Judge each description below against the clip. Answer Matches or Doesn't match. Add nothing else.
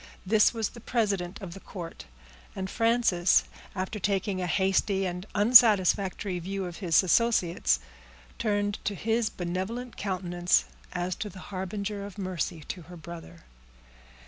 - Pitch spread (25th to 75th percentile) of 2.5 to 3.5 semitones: Matches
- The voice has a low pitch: Doesn't match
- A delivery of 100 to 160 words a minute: Matches